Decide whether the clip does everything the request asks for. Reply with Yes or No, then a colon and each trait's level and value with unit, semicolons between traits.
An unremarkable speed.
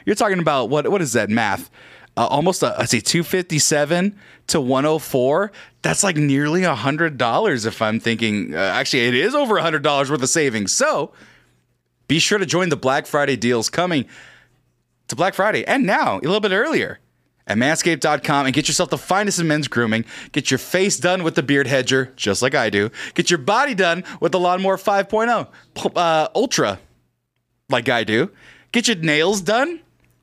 Yes: average, 185 wpm